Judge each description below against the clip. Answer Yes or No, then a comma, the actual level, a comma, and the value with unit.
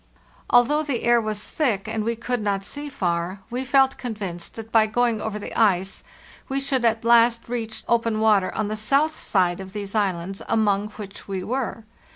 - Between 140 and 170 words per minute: No, average, 190 wpm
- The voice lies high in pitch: Yes, high, 220 Hz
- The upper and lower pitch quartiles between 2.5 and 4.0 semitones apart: Yes, average, 3.3 semitones